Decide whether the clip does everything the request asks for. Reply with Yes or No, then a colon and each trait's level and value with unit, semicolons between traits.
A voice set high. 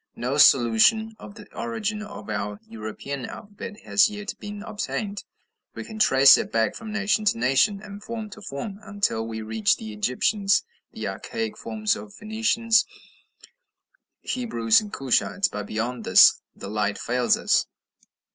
Yes: high, 200 Hz